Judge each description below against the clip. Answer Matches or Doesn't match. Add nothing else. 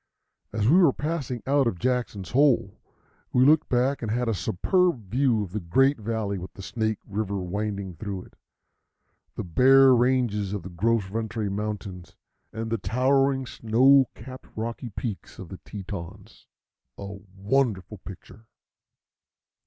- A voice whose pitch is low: Matches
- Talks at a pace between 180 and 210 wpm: Doesn't match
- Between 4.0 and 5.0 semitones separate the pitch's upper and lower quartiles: Matches